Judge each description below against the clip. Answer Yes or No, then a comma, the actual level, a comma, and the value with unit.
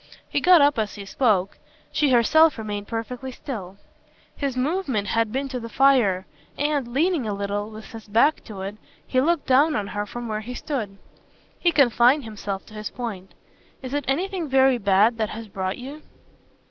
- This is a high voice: Yes, high, 240 Hz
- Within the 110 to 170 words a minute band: No, average, 185 wpm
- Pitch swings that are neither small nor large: Yes, average, 4.9 semitones